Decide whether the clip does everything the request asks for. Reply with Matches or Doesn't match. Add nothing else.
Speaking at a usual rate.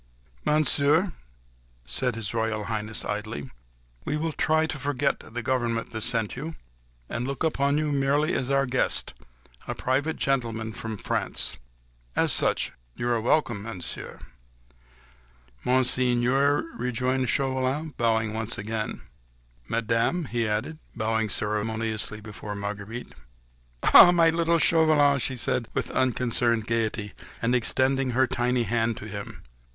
Doesn't match